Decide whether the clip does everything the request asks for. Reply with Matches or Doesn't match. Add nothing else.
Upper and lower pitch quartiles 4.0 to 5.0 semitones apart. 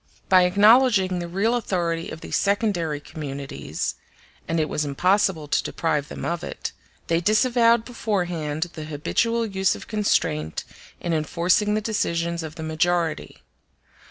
Matches